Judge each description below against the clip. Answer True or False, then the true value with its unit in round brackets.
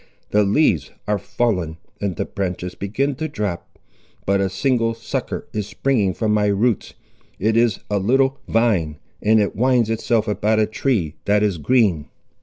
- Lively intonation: False (3.1 semitones)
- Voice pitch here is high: False (105 Hz)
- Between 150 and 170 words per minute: True (165 wpm)